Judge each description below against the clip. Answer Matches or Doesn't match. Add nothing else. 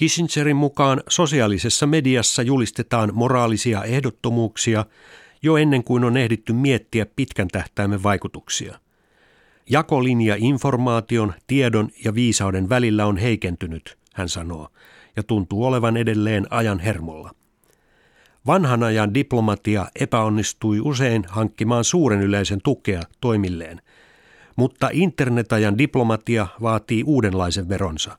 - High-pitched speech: Doesn't match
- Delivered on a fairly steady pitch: Doesn't match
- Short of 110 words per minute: Matches